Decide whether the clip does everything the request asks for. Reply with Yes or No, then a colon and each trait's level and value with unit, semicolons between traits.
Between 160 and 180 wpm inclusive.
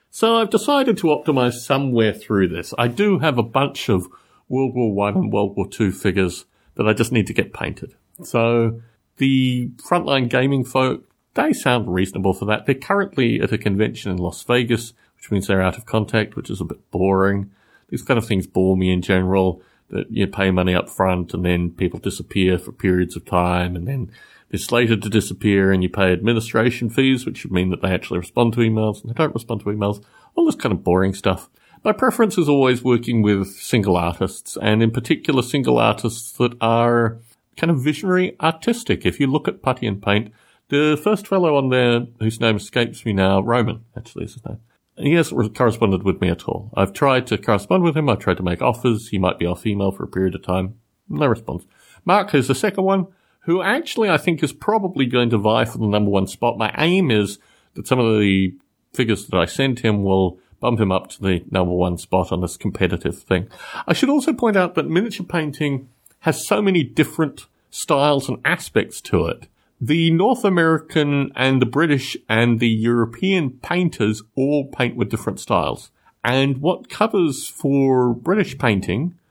No: average, 200 wpm